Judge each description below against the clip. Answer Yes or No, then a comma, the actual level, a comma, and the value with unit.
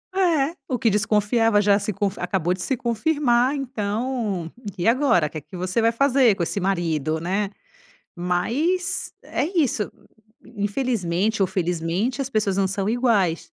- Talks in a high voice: Yes, high, 210 Hz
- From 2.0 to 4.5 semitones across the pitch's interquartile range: No, average, 5.3 semitones